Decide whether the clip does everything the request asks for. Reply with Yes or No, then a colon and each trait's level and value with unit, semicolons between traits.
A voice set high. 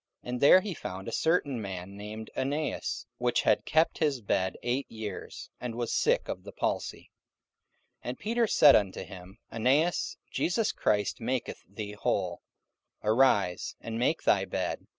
No: low, 115 Hz